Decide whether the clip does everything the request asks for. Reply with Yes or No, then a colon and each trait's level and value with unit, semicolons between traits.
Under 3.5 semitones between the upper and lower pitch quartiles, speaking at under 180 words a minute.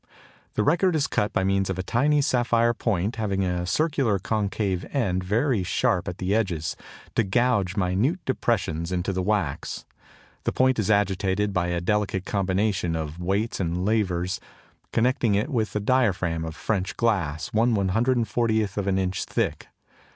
No: average, 3.9 semitones; average, 150 wpm